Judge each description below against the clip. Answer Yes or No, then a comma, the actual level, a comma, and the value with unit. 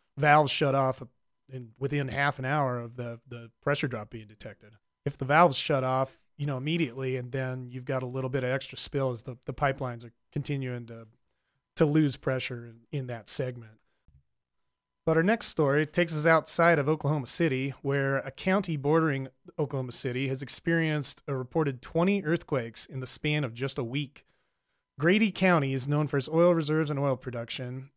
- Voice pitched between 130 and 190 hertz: Yes, low, 135 Hz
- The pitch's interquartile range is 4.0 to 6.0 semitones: No, average, 3.0 semitones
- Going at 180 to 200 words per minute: Yes, average, 185 wpm